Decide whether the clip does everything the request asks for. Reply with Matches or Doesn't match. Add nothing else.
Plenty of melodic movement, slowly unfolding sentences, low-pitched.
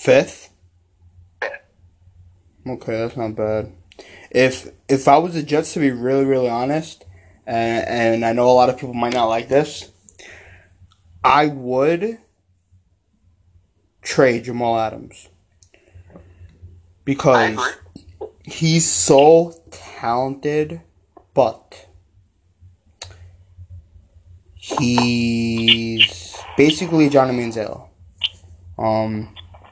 Matches